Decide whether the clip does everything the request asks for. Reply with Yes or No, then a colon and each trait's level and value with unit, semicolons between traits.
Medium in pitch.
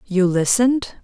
No: high, 205 Hz